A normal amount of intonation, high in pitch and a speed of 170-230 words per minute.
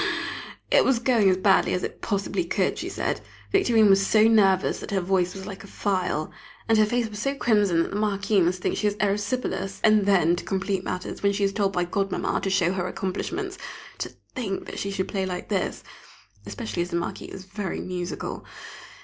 No: narrow, 2.3 semitones; high, 195 Hz; fast, 205 wpm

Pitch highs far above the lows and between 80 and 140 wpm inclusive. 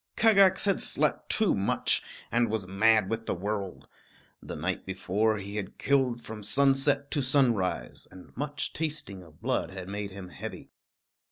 No: wide, 6.3 semitones; average, 160 wpm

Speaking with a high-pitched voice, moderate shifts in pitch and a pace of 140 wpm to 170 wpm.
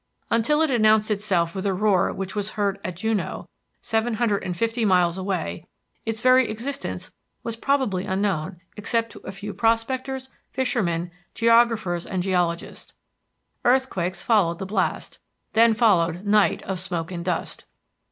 Yes: high, 205 Hz; average, 4.0 semitones; average, 145 wpm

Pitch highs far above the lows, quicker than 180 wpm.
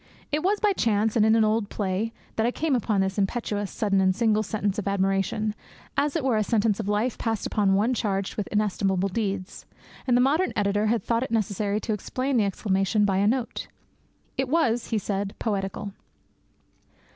No: average, 2.8 semitones; average, 190 wpm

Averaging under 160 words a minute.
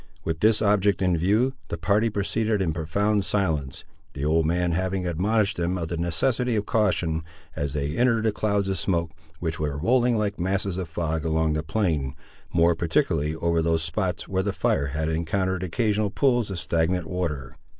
No: average, 180 wpm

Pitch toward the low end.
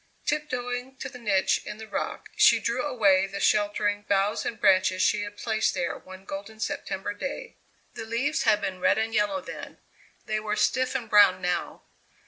No: high, 215 Hz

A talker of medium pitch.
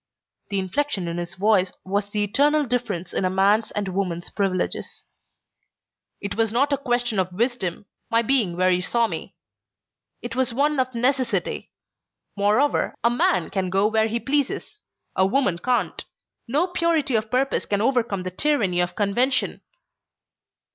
No: high, 220 Hz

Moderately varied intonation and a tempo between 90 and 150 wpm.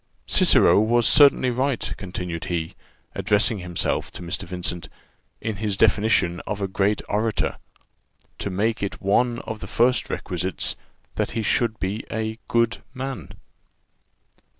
Yes: average, 3.6 semitones; slow, 135 wpm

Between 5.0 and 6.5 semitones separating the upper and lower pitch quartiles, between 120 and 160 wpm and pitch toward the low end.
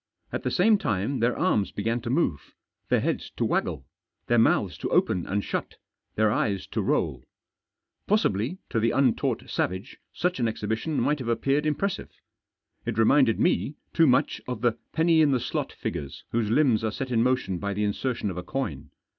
No: average, 5.3 semitones; average, 185 wpm; low, 120 Hz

